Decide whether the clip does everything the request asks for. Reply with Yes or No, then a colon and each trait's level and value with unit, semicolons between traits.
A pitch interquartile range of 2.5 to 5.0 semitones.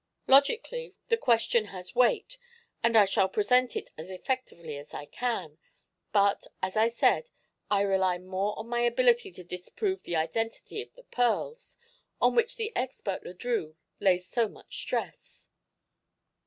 No: wide, 5.4 semitones